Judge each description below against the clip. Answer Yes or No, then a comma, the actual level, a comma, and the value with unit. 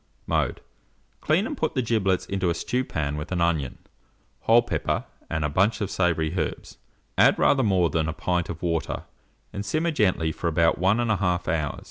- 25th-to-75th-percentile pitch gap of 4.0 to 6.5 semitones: Yes, average, 5.1 semitones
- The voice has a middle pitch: No, very low, 90 Hz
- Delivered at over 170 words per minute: Yes, average, 180 wpm